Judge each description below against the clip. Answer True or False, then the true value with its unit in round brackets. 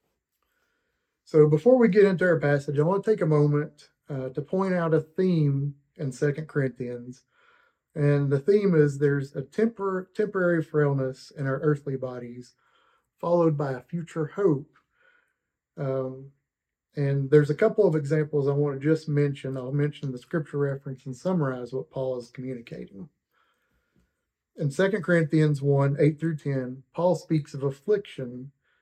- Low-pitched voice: False (150 Hz)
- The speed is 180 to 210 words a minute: False (155 wpm)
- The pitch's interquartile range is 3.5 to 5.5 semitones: True (4.0 semitones)